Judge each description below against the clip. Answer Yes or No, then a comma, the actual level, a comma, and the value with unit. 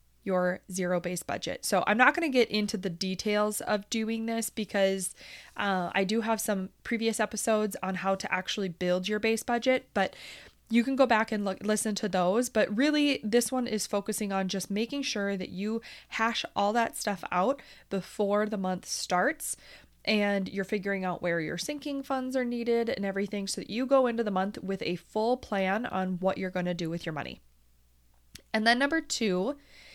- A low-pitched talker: No, high, 210 Hz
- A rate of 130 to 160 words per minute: No, average, 200 wpm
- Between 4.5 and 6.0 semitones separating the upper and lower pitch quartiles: No, average, 3.6 semitones